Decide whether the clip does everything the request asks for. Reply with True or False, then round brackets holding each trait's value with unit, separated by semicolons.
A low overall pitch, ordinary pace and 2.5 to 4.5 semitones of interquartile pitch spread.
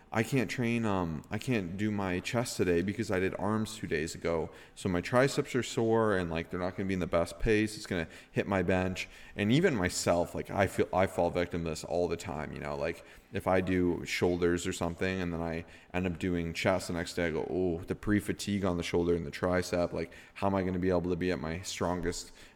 False (90 Hz; 250 wpm; 2.8 semitones)